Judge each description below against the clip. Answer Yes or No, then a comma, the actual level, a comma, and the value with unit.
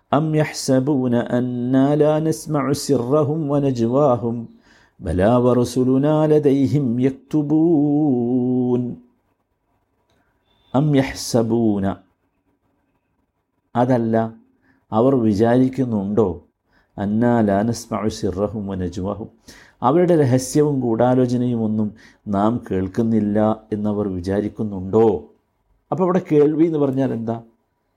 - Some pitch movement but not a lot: Yes, average, 4.3 semitones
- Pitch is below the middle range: Yes, low, 120 Hz